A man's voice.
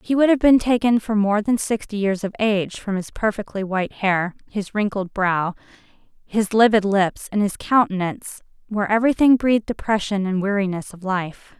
No: female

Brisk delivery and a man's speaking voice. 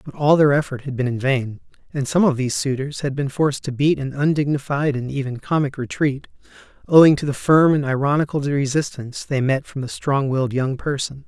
Yes: fast, 210 wpm; male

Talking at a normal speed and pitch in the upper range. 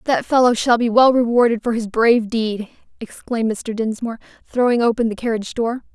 Yes: average, 180 wpm; high, 230 Hz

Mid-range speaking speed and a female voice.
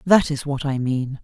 No: fast, 245 wpm; female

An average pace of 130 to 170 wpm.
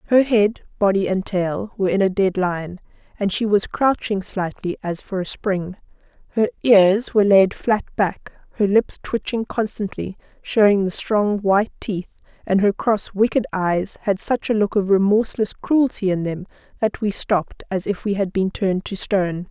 No: average, 180 wpm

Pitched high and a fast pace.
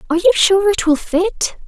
Yes: very high, 350 Hz; fast, 215 wpm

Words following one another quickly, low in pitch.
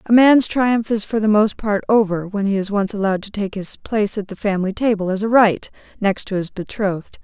No: fast, 240 wpm; high, 205 Hz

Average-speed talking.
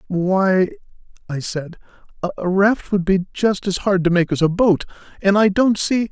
Yes: average, 185 wpm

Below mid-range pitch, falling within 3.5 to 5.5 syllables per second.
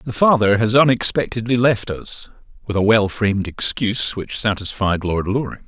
Yes: low, 110 Hz; 5.0 syllables/s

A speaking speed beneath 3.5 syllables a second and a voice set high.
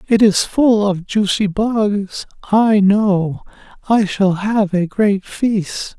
Yes: 2.9 syllables/s; high, 205 Hz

